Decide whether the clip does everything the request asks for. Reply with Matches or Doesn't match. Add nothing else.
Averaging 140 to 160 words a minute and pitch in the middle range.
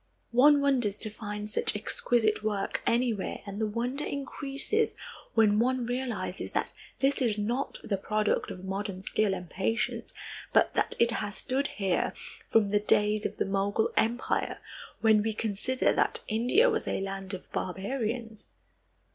Doesn't match